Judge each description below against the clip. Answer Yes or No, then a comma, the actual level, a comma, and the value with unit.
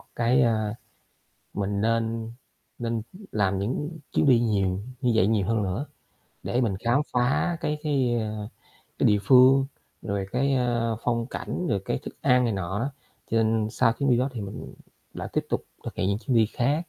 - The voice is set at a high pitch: No, low, 115 Hz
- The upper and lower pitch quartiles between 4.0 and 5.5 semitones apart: No, average, 3.2 semitones